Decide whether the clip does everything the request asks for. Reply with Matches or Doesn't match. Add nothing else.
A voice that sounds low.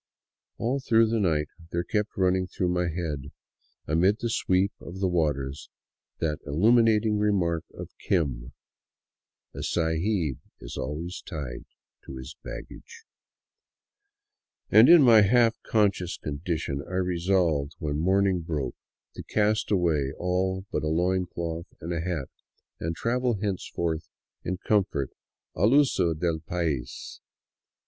Matches